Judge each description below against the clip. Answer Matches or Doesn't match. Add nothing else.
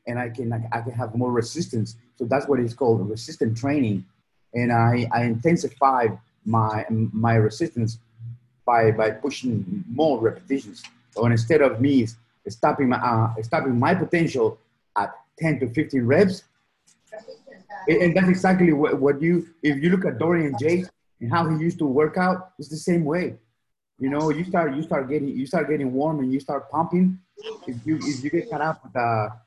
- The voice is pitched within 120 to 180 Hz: Matches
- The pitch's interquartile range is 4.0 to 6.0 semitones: Matches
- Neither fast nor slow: Matches